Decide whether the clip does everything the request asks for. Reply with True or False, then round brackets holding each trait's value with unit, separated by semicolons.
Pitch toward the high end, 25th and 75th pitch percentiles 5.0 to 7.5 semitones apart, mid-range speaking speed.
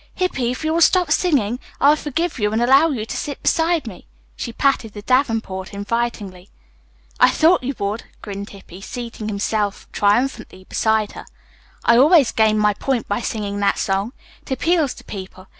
True (230 Hz; 5.3 semitones; 175 wpm)